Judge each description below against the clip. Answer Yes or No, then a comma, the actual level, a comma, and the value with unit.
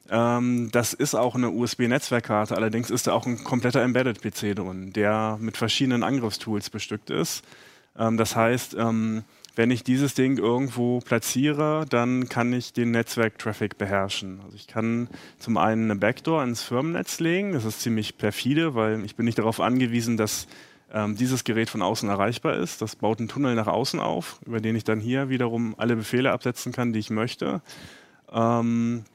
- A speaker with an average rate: Yes, average, 165 wpm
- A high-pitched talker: No, low, 115 Hz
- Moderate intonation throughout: No, narrow, 2.2 semitones